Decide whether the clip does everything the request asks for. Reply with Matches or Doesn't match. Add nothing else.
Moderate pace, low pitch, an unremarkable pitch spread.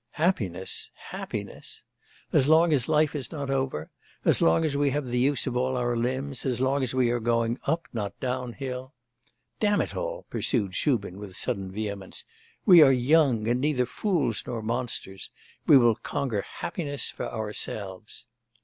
Matches